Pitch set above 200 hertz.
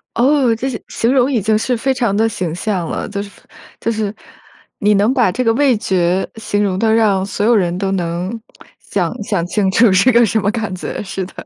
Yes: high, 210 Hz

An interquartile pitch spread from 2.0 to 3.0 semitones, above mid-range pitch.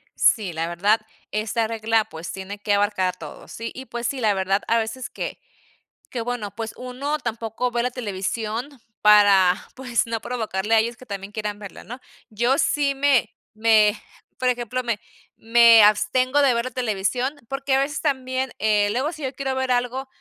No: average, 3.4 semitones; high, 230 Hz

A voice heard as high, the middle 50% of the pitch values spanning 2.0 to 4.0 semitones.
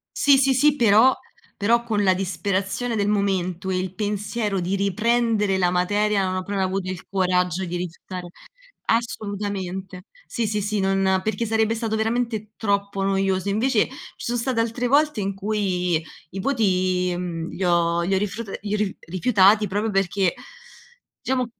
Yes: high, 200 Hz; average, 2.9 semitones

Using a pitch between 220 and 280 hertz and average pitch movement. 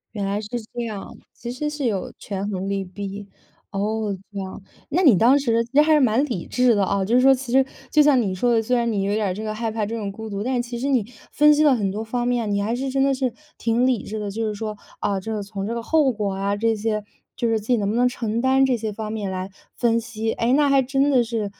Yes: high, 225 Hz; average, 3.6 semitones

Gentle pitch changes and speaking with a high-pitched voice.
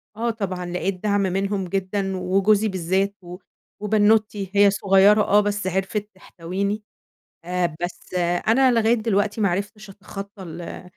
Yes: narrow, 2.1 semitones; high, 200 Hz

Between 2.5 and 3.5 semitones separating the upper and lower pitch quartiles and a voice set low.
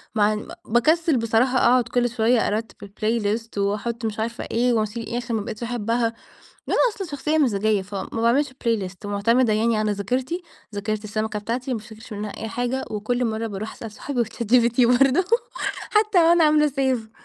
No: average, 2.8 semitones; high, 230 Hz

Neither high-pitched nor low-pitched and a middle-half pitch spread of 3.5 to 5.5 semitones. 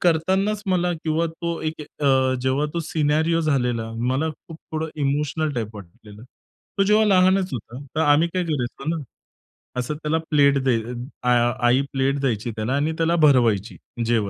Yes: medium, 145 Hz; average, 4.9 semitones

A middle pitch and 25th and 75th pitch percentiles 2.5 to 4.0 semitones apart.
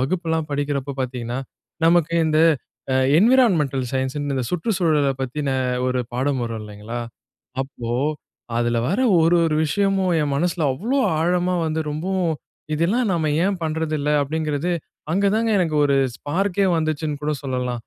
No: medium, 155 Hz; average, 4.6 semitones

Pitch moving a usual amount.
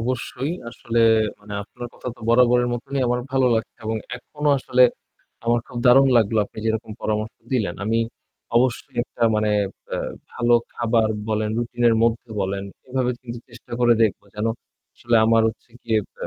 No: narrow, 1.7 semitones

